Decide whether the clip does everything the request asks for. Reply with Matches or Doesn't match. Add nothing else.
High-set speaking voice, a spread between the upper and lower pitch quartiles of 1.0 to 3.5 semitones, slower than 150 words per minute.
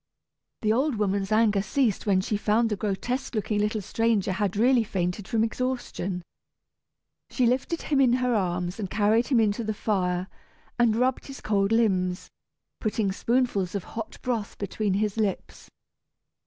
Doesn't match